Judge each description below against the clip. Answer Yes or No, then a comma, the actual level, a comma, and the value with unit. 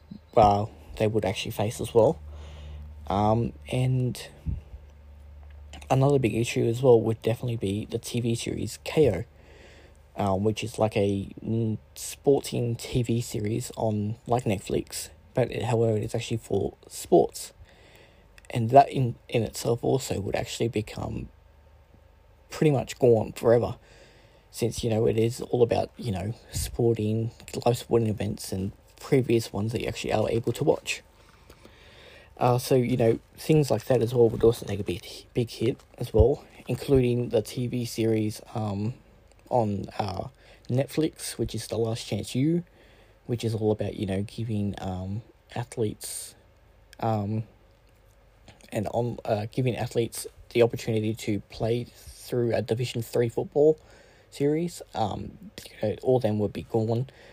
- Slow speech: No, average, 145 wpm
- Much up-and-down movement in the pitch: No, average, 3.2 semitones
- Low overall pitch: Yes, low, 110 Hz